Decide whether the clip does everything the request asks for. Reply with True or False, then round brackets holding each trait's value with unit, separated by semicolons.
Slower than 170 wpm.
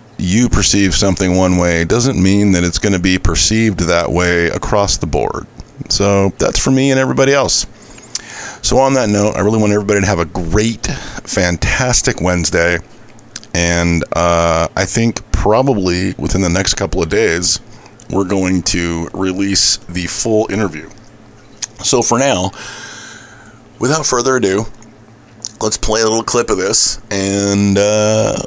True (150 wpm)